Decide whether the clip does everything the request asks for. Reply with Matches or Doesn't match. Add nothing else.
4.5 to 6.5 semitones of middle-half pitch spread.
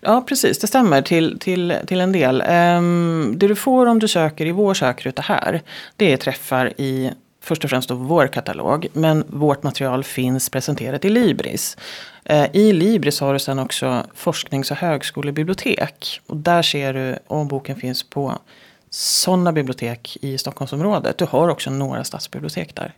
Matches